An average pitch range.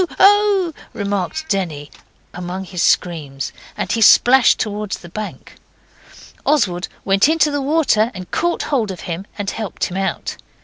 No: wide, 7.8 semitones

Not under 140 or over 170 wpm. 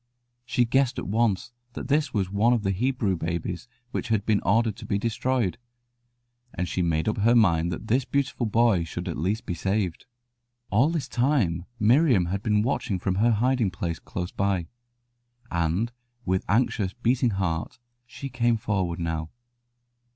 Yes: average, 165 wpm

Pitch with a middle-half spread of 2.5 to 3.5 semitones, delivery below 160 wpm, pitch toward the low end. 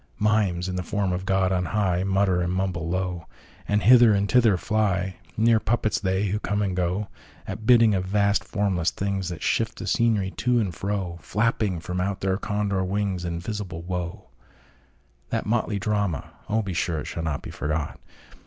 Yes: average, 2.8 semitones; average, 150 wpm; very low, 95 Hz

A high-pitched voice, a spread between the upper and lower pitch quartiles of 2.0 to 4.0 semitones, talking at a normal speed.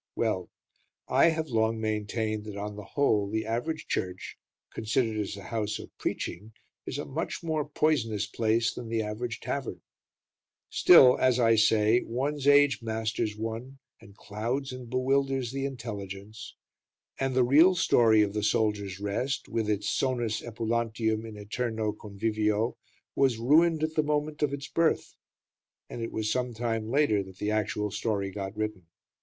No: low, 115 Hz; average, 3.7 semitones; average, 160 wpm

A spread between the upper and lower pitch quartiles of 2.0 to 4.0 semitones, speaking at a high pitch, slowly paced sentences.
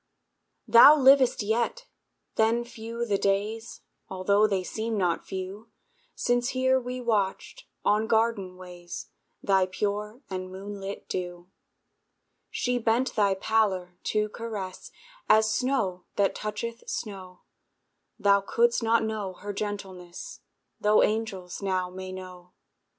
Yes: average, 3.5 semitones; high, 205 Hz; slow, 120 wpm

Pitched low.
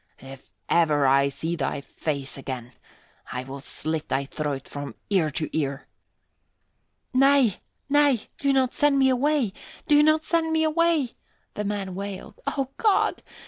No: high, 200 Hz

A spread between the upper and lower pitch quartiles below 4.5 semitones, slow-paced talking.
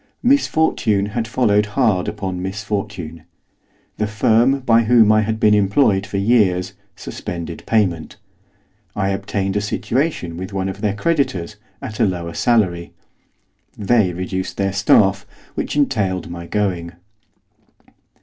Yes: average, 2.9 semitones; slow, 130 wpm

